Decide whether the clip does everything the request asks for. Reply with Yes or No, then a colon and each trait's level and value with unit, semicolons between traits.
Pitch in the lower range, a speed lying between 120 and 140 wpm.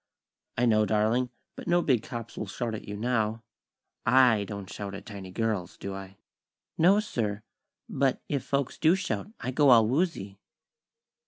No: low, 115 Hz; average, 165 wpm